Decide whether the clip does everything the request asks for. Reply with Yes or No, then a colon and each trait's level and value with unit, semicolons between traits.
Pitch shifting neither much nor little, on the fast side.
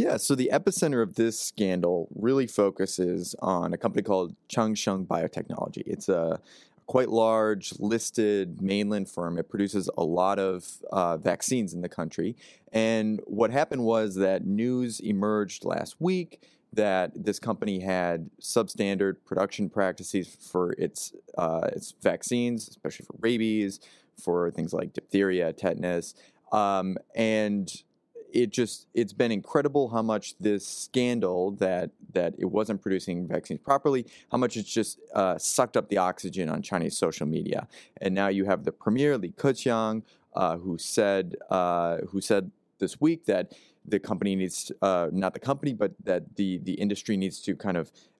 No: average, 3.5 semitones; average, 155 wpm